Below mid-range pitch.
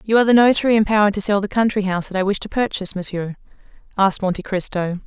No: high, 200 Hz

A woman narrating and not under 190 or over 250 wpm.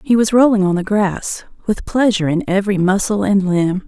Yes: female; average, 200 wpm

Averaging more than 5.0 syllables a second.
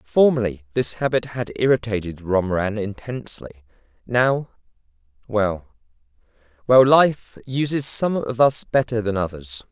No: 4.4 syllables/s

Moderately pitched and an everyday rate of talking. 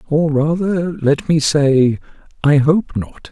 Yes: medium, 150 Hz; average, 145 wpm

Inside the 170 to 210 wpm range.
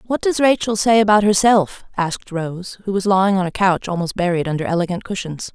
Yes: fast, 205 wpm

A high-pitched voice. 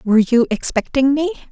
Yes: very high, 260 Hz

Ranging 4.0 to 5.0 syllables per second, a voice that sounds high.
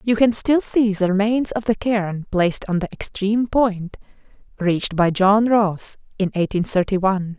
Yes: 4.7 syllables/s; high, 200 Hz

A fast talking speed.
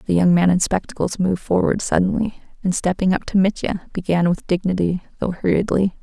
No: average, 180 wpm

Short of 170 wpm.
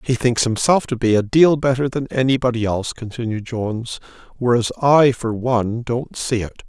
No: average, 180 wpm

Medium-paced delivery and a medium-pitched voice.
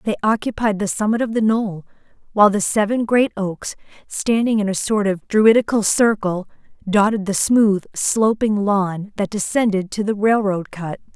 No: average, 160 wpm; high, 205 Hz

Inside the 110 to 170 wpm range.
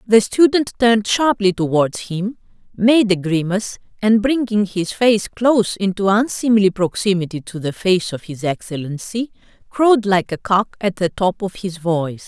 Yes: average, 160 wpm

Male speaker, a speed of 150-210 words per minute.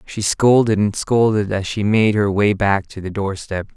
Yes: male; fast, 205 wpm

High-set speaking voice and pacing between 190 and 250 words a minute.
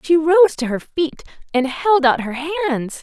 Yes: very high, 300 Hz; average, 200 wpm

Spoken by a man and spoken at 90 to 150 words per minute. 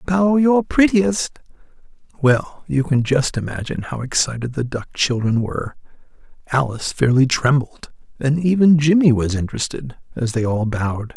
Yes: male; average, 140 wpm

